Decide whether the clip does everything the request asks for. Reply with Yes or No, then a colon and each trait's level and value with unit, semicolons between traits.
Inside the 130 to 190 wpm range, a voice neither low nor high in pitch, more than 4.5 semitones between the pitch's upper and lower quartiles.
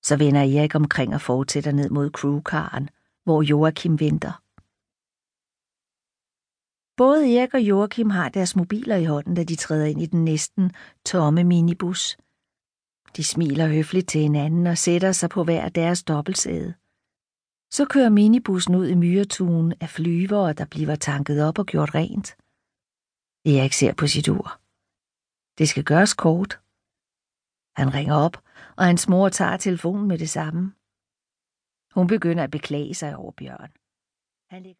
No: slow, 145 wpm; medium, 165 Hz; average, 3.8 semitones